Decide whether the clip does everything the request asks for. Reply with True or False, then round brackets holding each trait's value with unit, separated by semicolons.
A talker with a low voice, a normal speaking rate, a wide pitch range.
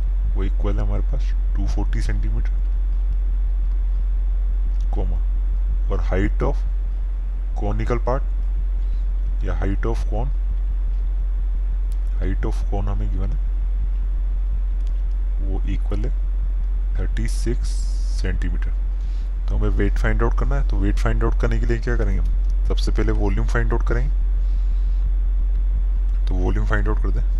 True (70 Hz; 120 wpm; 8.5 semitones)